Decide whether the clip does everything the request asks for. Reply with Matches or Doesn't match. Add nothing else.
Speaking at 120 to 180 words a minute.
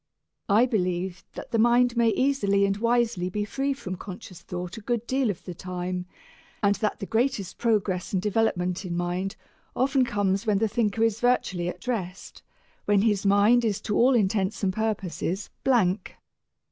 Matches